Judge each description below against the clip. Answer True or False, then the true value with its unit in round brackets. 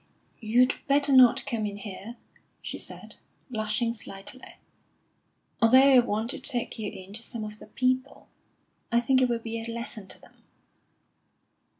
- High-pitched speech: True (235 Hz)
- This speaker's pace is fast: False (160 wpm)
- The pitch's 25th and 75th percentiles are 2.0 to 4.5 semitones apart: True (2.9 semitones)